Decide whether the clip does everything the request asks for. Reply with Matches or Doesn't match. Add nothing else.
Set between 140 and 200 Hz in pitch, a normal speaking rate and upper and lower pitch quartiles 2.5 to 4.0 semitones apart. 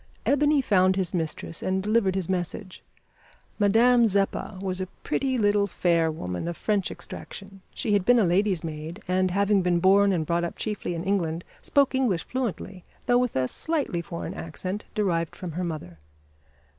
Matches